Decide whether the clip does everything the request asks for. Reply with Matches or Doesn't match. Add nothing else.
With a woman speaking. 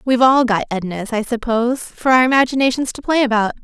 Matches